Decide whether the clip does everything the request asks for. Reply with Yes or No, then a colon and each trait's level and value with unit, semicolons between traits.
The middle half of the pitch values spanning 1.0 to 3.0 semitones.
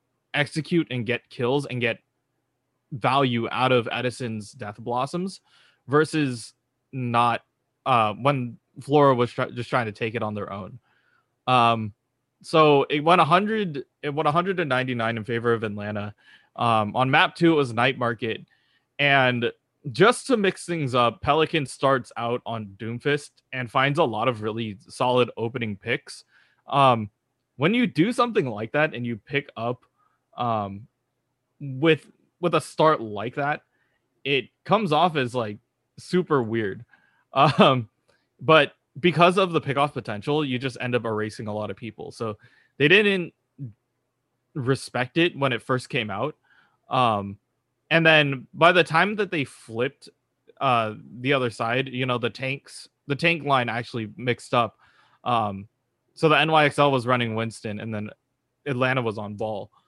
No: average, 3.7 semitones